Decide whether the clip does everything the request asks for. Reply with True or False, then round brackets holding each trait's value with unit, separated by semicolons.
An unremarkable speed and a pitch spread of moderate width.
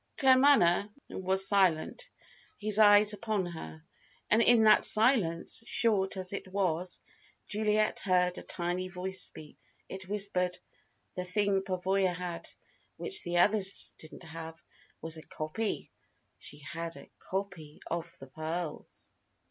False (130 wpm; 3.3 semitones)